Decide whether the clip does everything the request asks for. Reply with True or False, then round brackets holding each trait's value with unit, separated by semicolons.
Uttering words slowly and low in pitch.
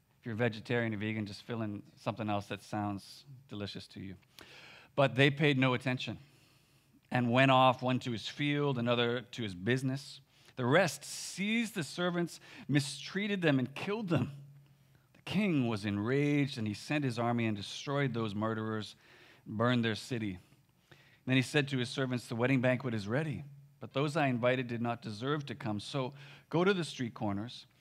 False (180 wpm; 130 Hz)